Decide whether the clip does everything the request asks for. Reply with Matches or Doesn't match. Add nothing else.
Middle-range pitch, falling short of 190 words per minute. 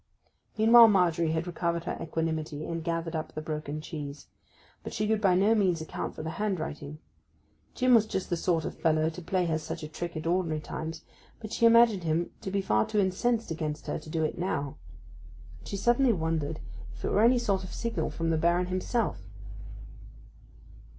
Doesn't match